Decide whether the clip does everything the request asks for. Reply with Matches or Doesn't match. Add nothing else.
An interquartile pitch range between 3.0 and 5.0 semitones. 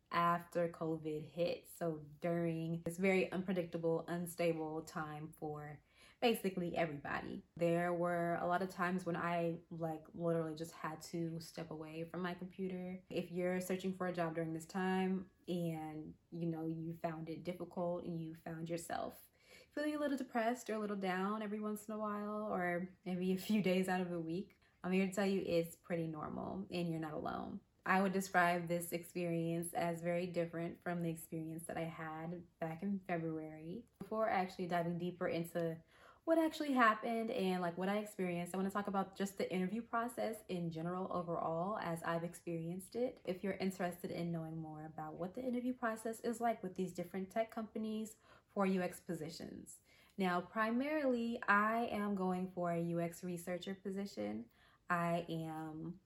Doesn't match